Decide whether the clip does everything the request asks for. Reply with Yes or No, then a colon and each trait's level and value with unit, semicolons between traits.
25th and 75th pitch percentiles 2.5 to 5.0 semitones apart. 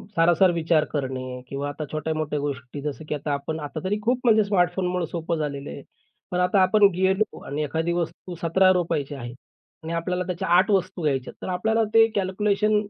Yes: average, 4.2 semitones